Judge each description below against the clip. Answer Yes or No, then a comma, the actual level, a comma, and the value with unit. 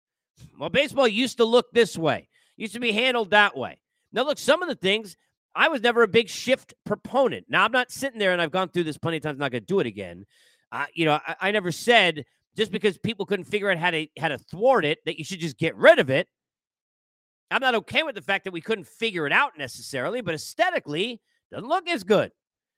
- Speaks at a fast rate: Yes, fast, 250 wpm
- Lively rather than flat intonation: Yes, wide, 6.5 semitones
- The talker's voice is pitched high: Yes, high, 205 Hz